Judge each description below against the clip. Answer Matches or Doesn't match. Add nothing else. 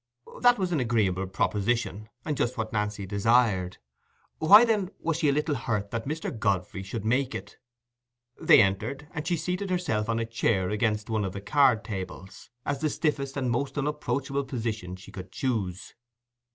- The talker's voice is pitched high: Doesn't match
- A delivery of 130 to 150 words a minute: Doesn't match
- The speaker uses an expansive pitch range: Matches